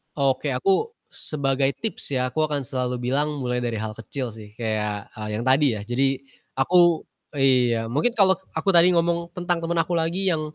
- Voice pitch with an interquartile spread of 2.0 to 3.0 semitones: No, wide, 5.5 semitones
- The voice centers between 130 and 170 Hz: Yes, low, 135 Hz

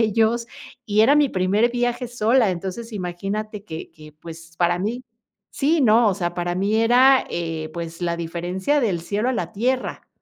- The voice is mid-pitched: No, high, 205 Hz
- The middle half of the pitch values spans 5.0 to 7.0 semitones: Yes, wide, 5.4 semitones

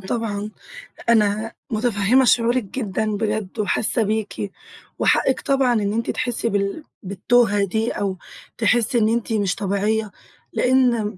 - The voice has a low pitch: No, high, 220 Hz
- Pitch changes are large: No, narrow, 2.6 semitones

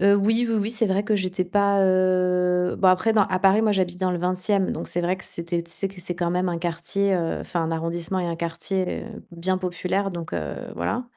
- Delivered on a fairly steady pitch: Yes, narrow, 2.2 semitones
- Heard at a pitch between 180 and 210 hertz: Yes, medium, 185 Hz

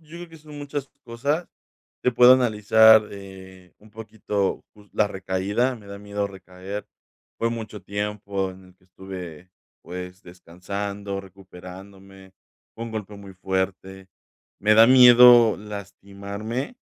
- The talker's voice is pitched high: No, low, 100 Hz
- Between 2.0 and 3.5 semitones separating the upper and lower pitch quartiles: Yes, average, 2.9 semitones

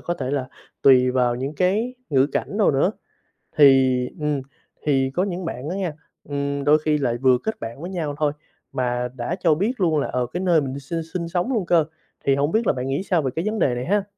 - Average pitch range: Yes, average, 5.0 semitones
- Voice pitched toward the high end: No, medium, 145 Hz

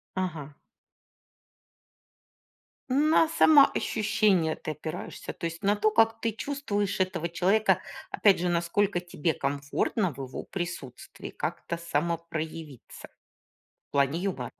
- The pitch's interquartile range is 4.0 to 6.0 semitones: Yes, average, 4.7 semitones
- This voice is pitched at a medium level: Yes, medium, 175 Hz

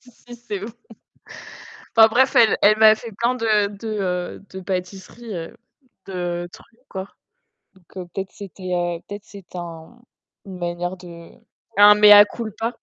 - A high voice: Yes, high, 200 Hz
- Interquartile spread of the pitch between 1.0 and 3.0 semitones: No, average, 3.6 semitones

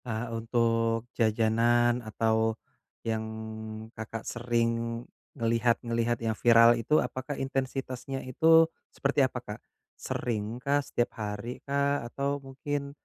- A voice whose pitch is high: No, low, 120 Hz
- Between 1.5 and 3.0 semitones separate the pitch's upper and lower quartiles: Yes, average, 2.7 semitones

